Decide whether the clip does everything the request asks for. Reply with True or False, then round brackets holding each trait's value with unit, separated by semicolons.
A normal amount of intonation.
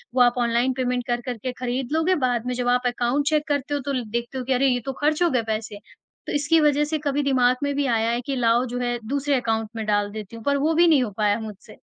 True (3.2 semitones)